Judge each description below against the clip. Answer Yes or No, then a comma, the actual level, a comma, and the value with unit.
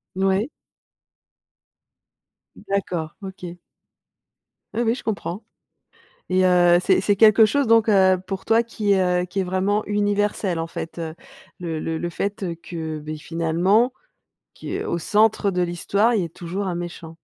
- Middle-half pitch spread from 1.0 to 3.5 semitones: Yes, average, 3.2 semitones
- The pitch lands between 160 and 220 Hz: Yes, high, 190 Hz